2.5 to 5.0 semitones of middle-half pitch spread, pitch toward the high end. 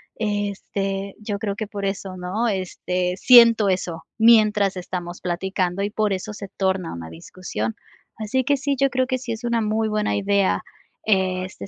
Yes: average, 2.9 semitones; high, 200 Hz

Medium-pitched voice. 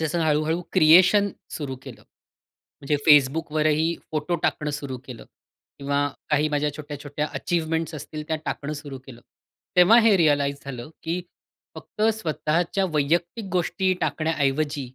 Yes: medium, 155 Hz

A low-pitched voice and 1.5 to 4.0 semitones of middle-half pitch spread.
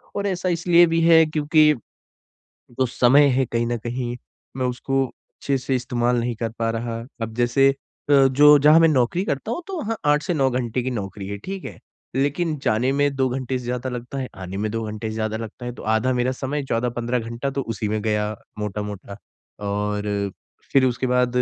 Yes: low, 125 Hz; average, 3.7 semitones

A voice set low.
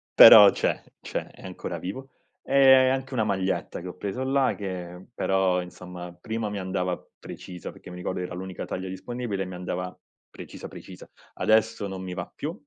Yes: very low, 95 Hz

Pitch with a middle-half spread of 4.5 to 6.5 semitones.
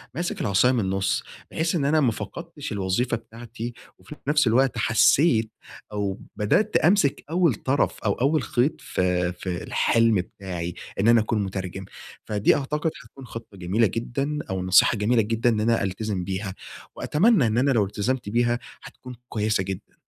Yes: average, 5.1 semitones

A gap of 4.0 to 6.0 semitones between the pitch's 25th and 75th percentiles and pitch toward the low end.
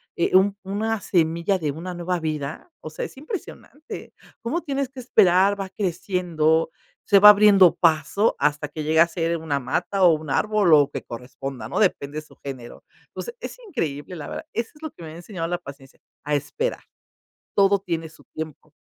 No: average, 4.7 semitones; medium, 175 Hz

